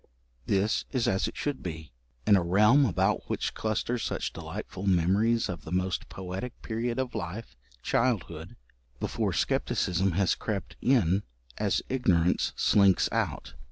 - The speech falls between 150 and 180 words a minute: No, average, 140 wpm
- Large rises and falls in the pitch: No, average, 4.3 semitones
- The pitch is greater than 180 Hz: No, low, 100 Hz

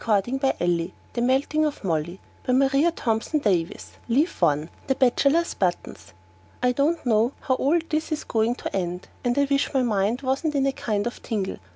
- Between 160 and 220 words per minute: Yes, average, 180 wpm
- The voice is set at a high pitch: Yes, very high, 250 Hz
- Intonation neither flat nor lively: No, wide, 5.7 semitones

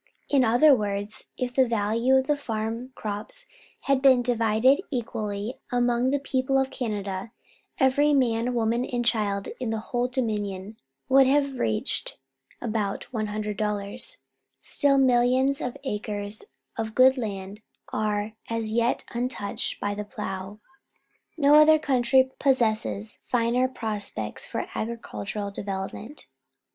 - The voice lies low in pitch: No, high, 230 Hz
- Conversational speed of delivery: No, slow, 125 wpm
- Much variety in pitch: No, average, 3.8 semitones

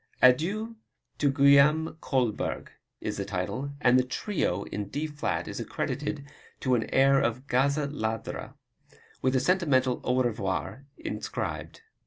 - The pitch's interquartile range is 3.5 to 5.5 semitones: No, average, 3.1 semitones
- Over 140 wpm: No, slow, 135 wpm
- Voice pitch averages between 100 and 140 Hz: Yes, low, 135 Hz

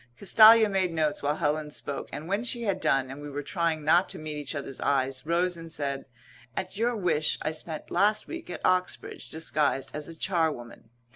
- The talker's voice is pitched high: No, medium, 160 Hz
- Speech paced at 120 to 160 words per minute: No, average, 200 wpm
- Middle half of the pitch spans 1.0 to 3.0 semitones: No, average, 4.3 semitones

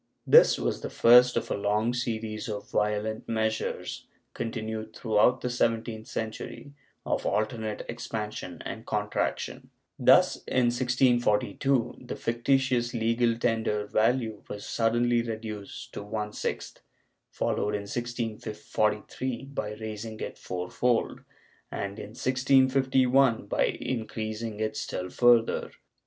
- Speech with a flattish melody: Yes, narrow, 2.2 semitones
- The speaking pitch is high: No, low, 115 Hz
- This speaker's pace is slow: Yes, slow, 115 wpm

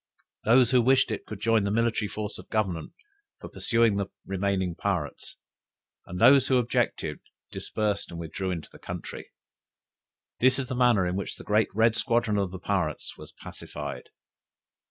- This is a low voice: Yes, low, 105 Hz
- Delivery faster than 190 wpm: No, average, 165 wpm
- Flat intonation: No, average, 3.7 semitones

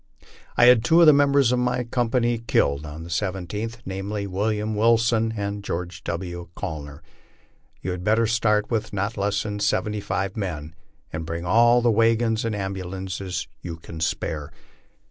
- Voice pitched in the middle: No, low, 105 Hz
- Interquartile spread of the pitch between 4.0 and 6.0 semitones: Yes, average, 4.4 semitones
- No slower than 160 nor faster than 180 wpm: Yes, average, 165 wpm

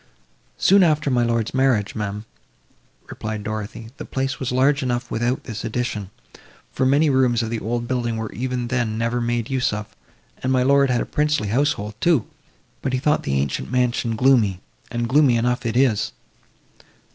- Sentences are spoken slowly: No, average, 175 wpm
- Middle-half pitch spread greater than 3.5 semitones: No, average, 2.9 semitones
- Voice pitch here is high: No, low, 120 Hz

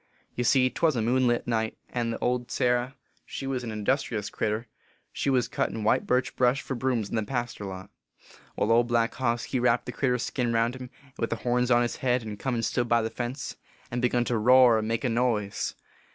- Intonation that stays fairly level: Yes, narrow, 1.7 semitones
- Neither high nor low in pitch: No, low, 120 Hz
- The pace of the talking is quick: Yes, fast, 225 wpm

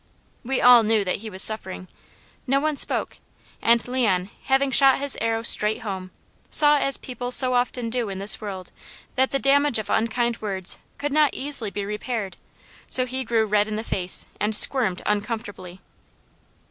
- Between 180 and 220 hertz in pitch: No, high, 230 Hz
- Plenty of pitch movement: No, average, 4.1 semitones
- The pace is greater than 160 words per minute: Yes, average, 170 wpm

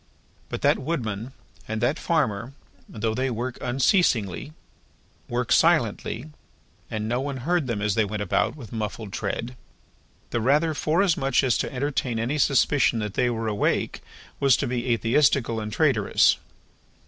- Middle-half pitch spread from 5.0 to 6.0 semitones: No, average, 3.9 semitones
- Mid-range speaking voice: No, low, 120 Hz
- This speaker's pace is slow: No, average, 150 wpm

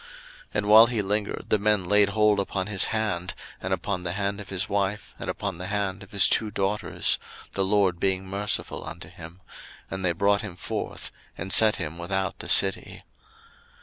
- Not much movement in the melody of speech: Yes, narrow, 1.7 semitones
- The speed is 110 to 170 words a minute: No, average, 190 wpm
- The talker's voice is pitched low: Yes, low, 100 Hz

